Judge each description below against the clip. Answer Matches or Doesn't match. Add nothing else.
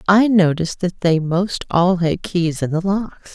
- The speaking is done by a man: Doesn't match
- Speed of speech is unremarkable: Matches